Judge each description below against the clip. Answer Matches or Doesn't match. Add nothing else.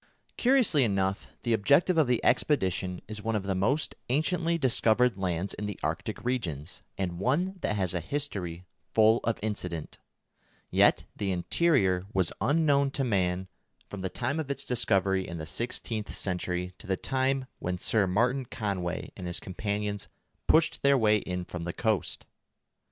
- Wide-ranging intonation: Matches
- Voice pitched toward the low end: Matches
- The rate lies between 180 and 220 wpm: Doesn't match